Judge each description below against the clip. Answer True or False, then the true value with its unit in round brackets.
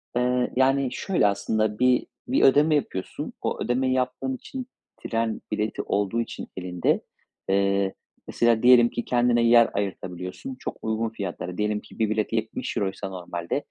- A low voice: True (115 Hz)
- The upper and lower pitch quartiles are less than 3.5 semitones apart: False (4.0 semitones)